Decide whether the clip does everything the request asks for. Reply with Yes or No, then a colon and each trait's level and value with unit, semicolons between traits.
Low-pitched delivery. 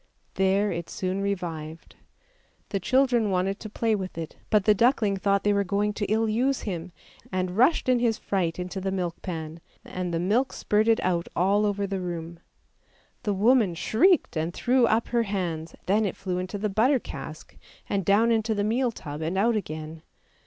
No: high, 200 Hz